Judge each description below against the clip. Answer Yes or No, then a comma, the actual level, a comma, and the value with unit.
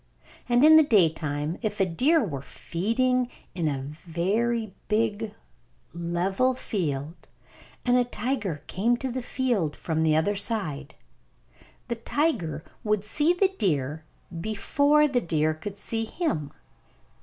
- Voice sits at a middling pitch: No, high, 205 Hz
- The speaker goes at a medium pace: No, slow, 130 wpm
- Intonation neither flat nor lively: No, wide, 7.4 semitones